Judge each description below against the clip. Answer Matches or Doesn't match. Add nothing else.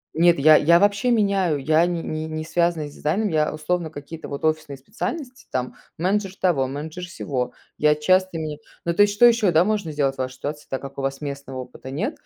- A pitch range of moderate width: Matches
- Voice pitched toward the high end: Doesn't match